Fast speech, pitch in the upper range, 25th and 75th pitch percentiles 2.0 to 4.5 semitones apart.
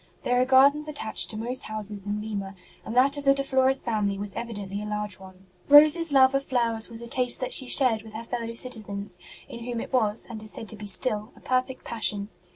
Yes: fast, 240 wpm; high, 230 Hz; average, 3.8 semitones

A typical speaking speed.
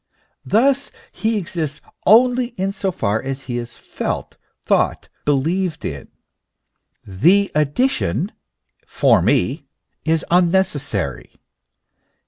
No: slow, 105 wpm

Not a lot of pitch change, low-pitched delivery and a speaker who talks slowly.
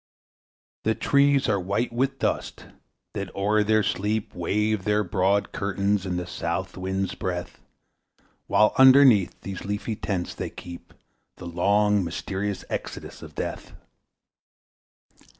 Yes: narrow, 2.3 semitones; low, 100 Hz; slow, 125 wpm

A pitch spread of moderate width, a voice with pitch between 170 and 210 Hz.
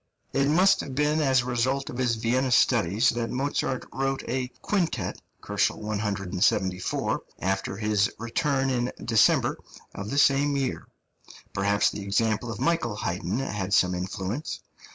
No: average, 4.9 semitones; low, 120 Hz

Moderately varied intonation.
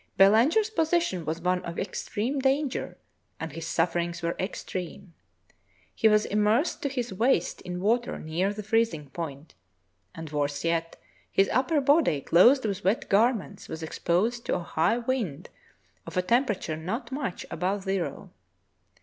No: wide, 6.1 semitones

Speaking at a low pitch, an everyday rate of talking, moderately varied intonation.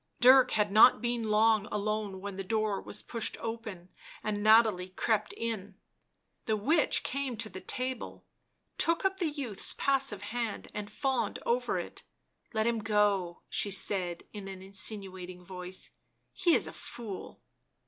No: high, 215 Hz; average, 160 wpm; average, 3.4 semitones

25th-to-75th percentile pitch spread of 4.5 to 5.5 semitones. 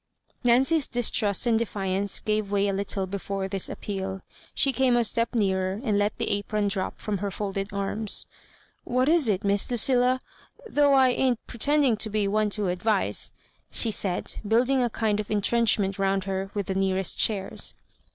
No: average, 3.4 semitones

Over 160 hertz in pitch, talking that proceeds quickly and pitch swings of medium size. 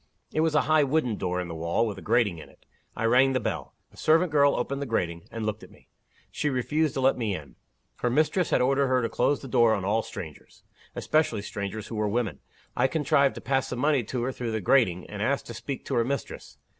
No: low, 120 Hz; fast, 245 wpm; average, 5.0 semitones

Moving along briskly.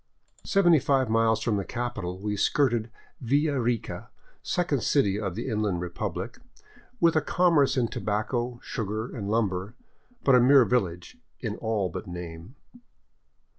No: average, 140 wpm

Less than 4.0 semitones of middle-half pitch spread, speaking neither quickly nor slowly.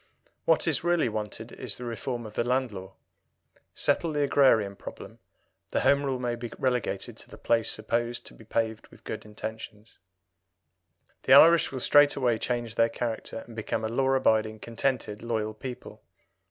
Yes: average, 3.1 semitones; average, 165 wpm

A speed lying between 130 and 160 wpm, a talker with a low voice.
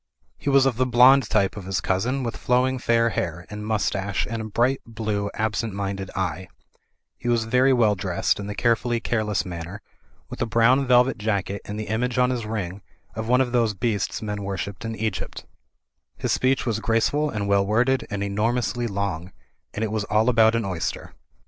No: average, 200 wpm; low, 110 Hz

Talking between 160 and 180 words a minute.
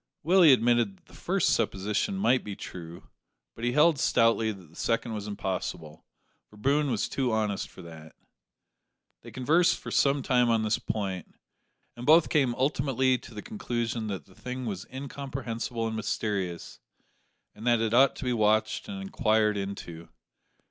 Yes: average, 165 wpm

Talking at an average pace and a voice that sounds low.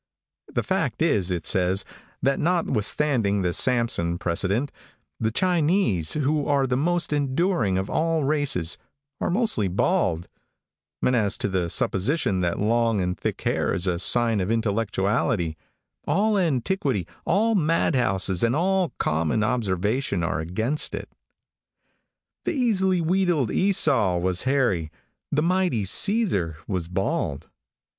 No: slow, 130 wpm; low, 115 Hz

